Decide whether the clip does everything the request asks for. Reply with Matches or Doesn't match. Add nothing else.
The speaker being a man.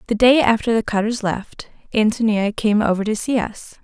Doesn't match